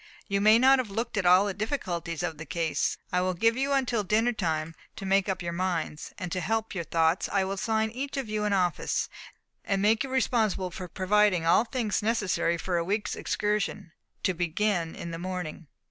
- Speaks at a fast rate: Yes, fast, 210 wpm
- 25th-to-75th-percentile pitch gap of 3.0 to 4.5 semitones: Yes, average, 3.9 semitones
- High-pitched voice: Yes, high, 195 Hz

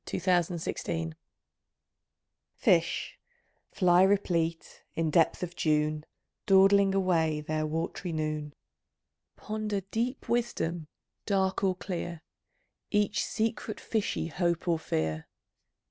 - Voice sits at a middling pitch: Yes, medium, 175 Hz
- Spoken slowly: Yes, slow, 100 wpm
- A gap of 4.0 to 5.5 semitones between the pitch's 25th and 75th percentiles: No, average, 3.6 semitones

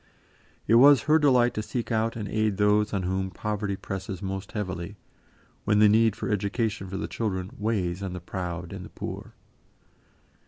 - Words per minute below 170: No, average, 180 wpm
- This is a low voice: Yes, low, 105 Hz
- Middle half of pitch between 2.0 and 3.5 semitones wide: Yes, average, 2.7 semitones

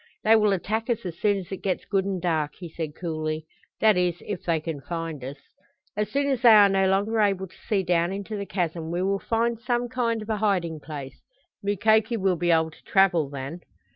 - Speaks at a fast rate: Yes, fast, 225 wpm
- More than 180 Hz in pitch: Yes, high, 190 Hz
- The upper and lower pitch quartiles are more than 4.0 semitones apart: Yes, average, 4.4 semitones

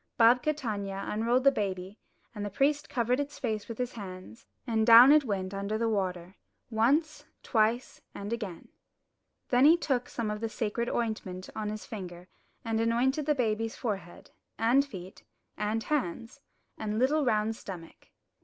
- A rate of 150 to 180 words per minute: Yes, average, 160 wpm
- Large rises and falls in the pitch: No, average, 3.5 semitones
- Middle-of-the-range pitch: No, high, 225 Hz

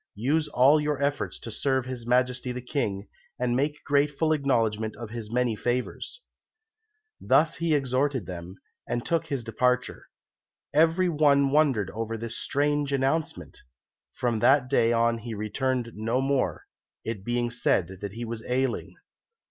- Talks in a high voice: No, low, 125 Hz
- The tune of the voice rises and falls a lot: No, average, 3.7 semitones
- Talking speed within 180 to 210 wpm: No, average, 150 wpm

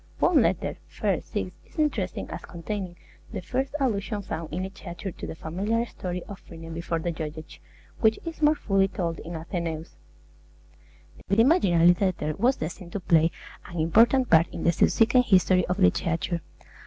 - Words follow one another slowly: No, average, 165 wpm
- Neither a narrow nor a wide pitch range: Yes, average, 4.6 semitones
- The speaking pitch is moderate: Yes, medium, 180 Hz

